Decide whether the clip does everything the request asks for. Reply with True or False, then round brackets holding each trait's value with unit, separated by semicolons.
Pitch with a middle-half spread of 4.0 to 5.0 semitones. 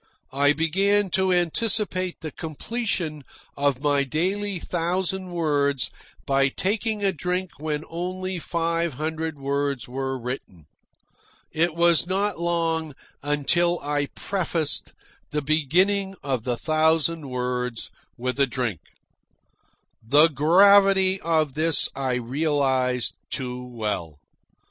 True (4.7 semitones)